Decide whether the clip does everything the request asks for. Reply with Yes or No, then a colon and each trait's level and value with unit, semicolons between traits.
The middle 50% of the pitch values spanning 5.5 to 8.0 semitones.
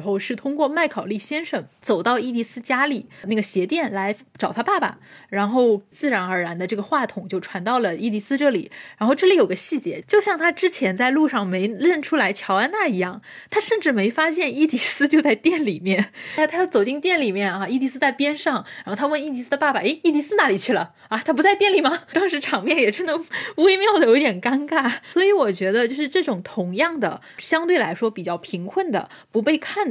Yes: wide, 7.5 semitones